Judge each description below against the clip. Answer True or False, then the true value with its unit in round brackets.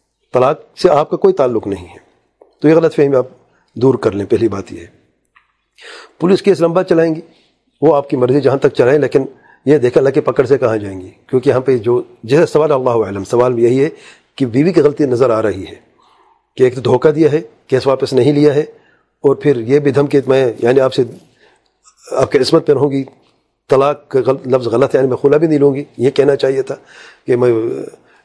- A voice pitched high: False (140 Hz)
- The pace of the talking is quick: True (225 wpm)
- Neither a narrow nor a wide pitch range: True (4.1 semitones)